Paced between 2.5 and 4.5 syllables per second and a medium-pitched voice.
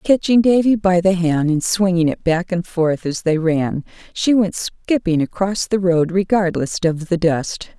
Yes: 4.4 syllables/s; medium, 180 Hz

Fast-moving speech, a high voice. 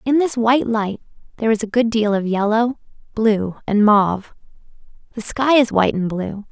No: average, 185 wpm; high, 220 Hz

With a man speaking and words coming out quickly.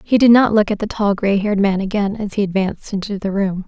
No: female; fast, 275 wpm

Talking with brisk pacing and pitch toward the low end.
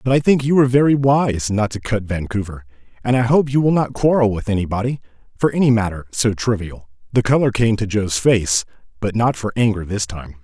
Yes: fast, 215 wpm; low, 115 Hz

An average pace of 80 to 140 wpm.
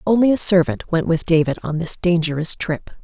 No: average, 200 wpm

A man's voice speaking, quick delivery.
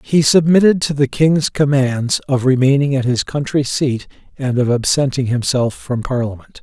No: male; average, 165 wpm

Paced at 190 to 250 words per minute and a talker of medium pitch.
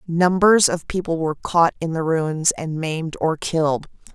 No: average, 175 wpm; medium, 165 Hz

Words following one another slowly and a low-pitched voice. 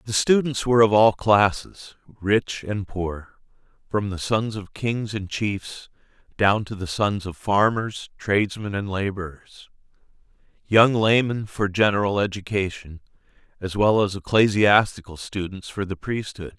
Yes: slow, 130 wpm; low, 100 Hz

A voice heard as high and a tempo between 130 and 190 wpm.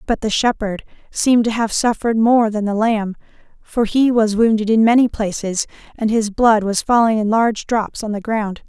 No: high, 220 Hz; average, 200 wpm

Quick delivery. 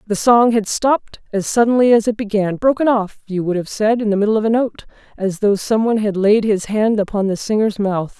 Yes: fast, 225 wpm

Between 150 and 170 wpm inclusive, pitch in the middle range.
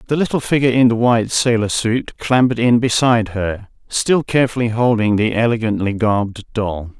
No: average, 165 wpm; low, 115 Hz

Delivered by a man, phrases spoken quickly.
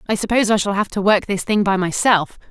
No: female; fast, 265 wpm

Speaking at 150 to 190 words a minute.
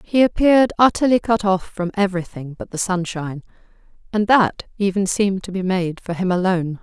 Yes: average, 175 wpm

